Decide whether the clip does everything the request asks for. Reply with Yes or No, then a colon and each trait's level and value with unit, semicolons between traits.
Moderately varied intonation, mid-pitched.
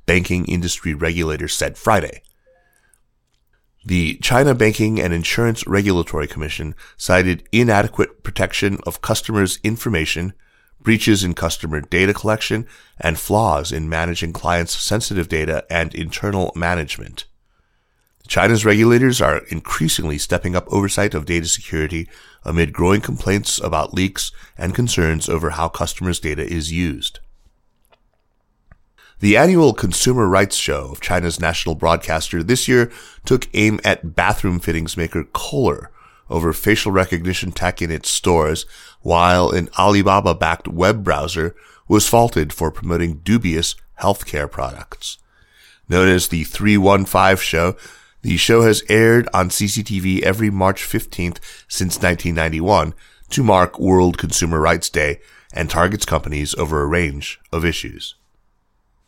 No: average, 3.9 semitones; very low, 90 Hz